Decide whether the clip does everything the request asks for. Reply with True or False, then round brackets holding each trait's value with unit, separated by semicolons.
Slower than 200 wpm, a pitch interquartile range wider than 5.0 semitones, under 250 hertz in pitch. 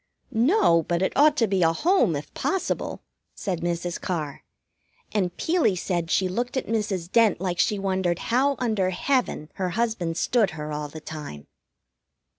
True (165 wpm; 5.4 semitones; 185 Hz)